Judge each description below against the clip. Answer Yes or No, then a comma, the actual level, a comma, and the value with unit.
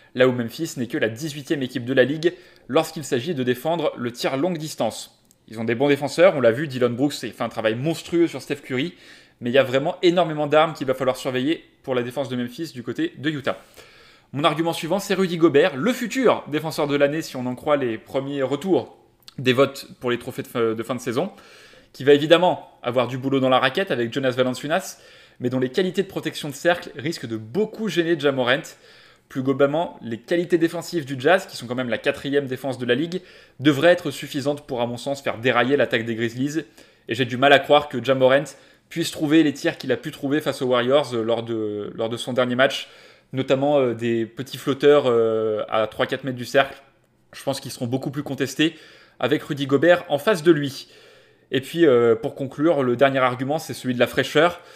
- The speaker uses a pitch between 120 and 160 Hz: Yes, medium, 140 Hz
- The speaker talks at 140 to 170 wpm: No, fast, 220 wpm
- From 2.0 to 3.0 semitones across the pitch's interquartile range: No, average, 4.0 semitones